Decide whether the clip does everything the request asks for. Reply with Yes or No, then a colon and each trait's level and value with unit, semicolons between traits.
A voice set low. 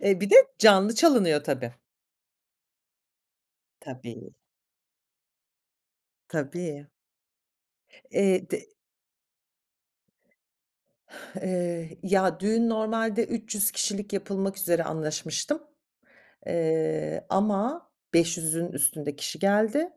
No: high, 190 Hz